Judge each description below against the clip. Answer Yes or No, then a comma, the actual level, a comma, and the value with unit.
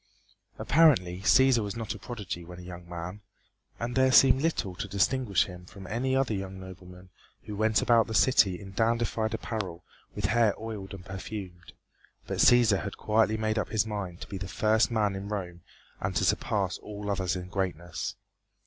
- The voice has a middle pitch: No, low, 100 Hz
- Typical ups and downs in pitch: Yes, average, 3.5 semitones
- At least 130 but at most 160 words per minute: No, average, 185 wpm